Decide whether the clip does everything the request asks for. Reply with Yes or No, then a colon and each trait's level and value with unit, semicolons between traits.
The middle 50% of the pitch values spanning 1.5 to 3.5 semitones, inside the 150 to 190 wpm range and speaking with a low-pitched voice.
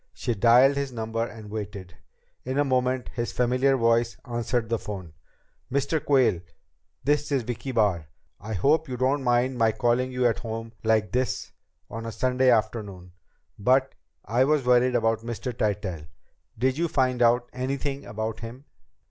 Yes: average, 2.7 semitones; average, 160 wpm; low, 120 Hz